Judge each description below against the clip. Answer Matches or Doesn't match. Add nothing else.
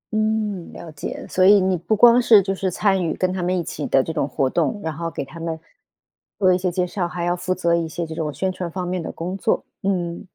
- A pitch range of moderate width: Doesn't match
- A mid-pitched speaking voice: Matches